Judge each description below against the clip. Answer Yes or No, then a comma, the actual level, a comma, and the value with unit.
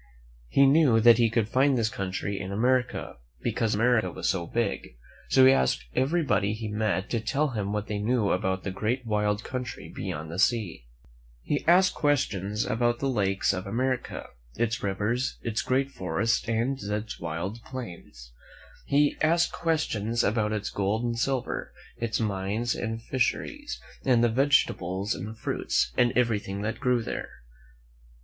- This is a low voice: Yes, low, 115 Hz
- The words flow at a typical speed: Yes, average, 155 wpm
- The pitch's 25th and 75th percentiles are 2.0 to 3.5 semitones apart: No, average, 3.9 semitones